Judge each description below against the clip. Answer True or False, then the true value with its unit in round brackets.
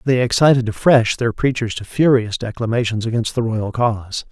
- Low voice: True (115 Hz)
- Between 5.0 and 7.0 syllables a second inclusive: True (5.3 syllables/s)